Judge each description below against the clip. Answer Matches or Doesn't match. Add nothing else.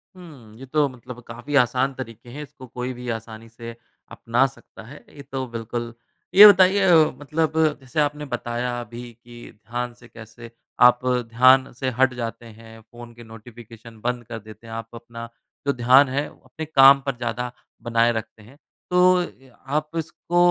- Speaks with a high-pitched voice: Doesn't match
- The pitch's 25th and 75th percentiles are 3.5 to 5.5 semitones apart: Doesn't match